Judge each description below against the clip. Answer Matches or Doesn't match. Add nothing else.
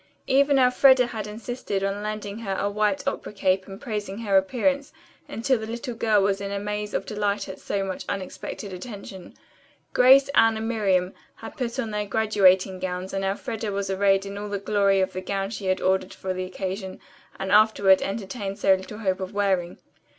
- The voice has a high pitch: Matches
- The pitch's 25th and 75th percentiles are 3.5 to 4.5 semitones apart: Doesn't match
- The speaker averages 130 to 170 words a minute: Doesn't match